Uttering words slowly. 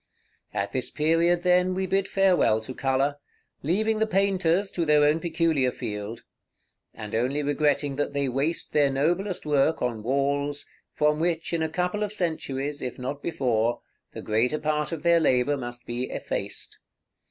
No: average, 165 wpm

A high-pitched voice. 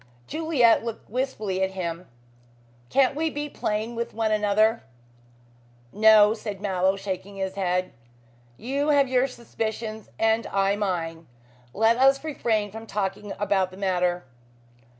Yes: high, 215 Hz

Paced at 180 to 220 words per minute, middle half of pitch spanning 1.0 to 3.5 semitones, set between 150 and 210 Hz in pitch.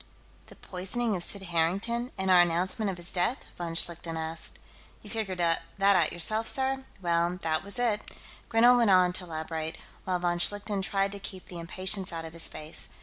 Yes: average, 190 wpm; average, 3.1 semitones; medium, 185 Hz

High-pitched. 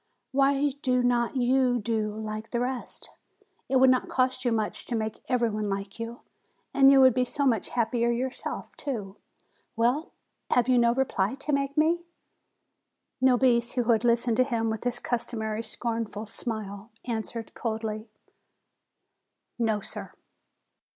Yes: high, 235 Hz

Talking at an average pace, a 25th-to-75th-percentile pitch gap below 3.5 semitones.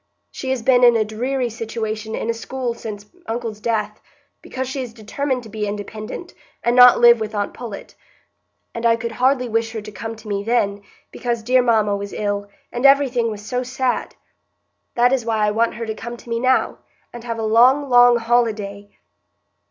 Yes: average, 195 wpm; narrow, 2.4 semitones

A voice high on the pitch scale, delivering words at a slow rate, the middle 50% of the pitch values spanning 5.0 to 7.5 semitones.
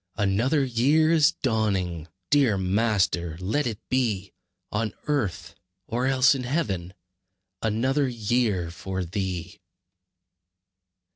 No: low, 110 Hz; slow, 100 wpm; wide, 5.6 semitones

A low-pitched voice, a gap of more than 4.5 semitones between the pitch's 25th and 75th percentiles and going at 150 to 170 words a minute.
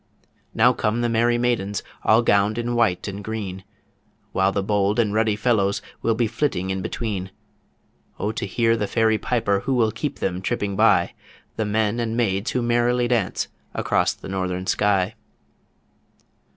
No: low, 110 Hz; average, 3.2 semitones; average, 165 wpm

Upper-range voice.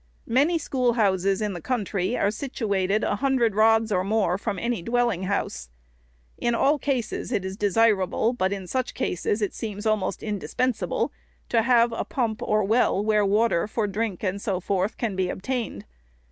Yes: high, 215 Hz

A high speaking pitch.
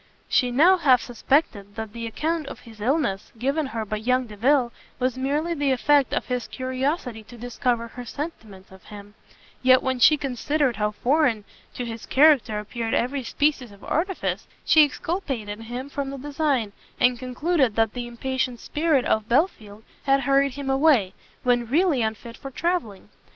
Yes: very high, 255 Hz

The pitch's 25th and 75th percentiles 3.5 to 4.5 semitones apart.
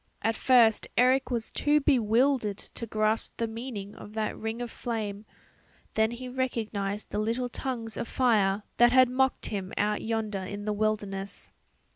No: average, 2.9 semitones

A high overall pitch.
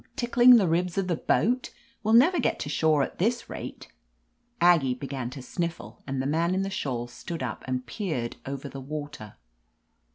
No: medium, 160 Hz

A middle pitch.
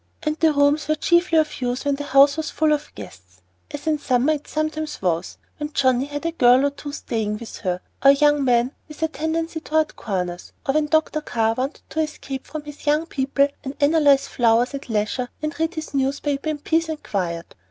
No: very high, 285 Hz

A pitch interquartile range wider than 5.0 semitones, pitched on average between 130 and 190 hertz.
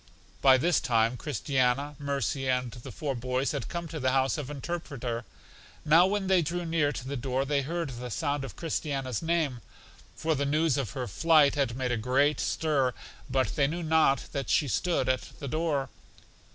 No: average, 3.5 semitones; medium, 140 Hz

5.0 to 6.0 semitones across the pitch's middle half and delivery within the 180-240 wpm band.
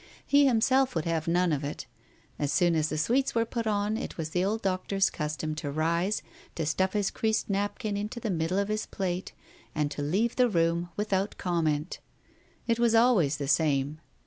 Yes: wide, 5.5 semitones; average, 195 wpm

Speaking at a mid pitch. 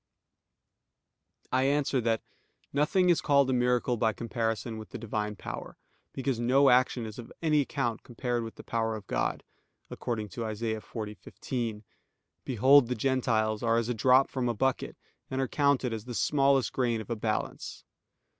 No: low, 120 Hz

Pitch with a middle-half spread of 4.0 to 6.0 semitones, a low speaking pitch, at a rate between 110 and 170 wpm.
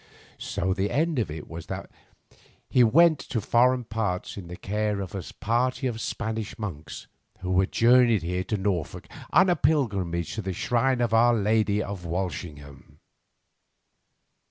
Yes: average, 4.7 semitones; low, 105 Hz; average, 155 wpm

